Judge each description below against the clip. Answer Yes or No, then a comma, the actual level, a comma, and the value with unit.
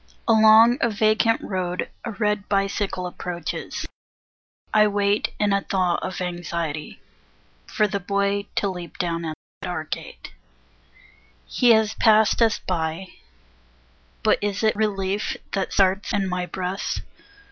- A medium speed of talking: No, slow, 130 wpm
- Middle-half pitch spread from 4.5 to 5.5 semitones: No, average, 2.8 semitones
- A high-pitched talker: Yes, high, 200 Hz